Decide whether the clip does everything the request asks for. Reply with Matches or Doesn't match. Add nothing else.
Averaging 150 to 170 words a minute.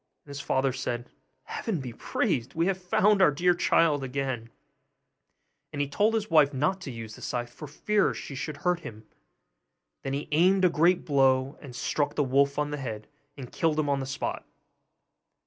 Doesn't match